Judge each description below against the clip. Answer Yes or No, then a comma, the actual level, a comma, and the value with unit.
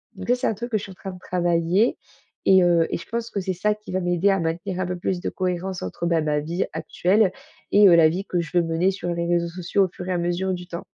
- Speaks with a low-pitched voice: No, medium, 180 Hz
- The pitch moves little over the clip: Yes, narrow, 2.1 semitones